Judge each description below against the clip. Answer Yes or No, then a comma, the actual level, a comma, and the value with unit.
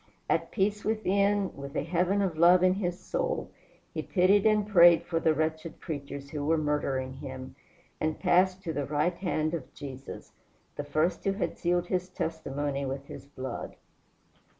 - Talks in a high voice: No, medium, 165 Hz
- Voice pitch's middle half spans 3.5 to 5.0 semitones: Yes, average, 4.3 semitones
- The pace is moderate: Yes, average, 170 wpm